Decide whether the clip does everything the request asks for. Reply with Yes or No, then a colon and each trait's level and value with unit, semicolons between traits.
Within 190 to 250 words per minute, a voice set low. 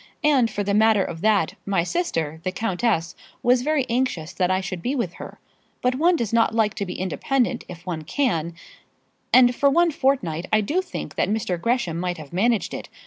No: average, 195 wpm; high, 215 Hz